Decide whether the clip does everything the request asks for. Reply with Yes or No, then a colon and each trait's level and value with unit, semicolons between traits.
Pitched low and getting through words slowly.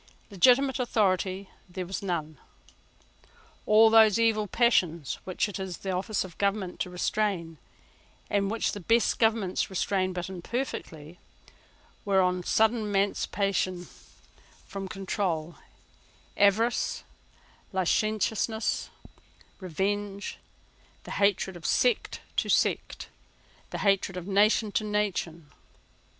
No: high, 195 Hz; slow, 110 wpm